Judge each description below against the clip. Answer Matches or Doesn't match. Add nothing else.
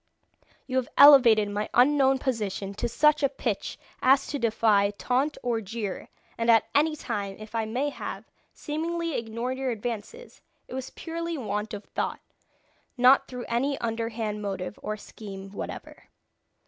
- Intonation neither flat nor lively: Matches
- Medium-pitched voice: Doesn't match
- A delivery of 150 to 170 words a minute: Matches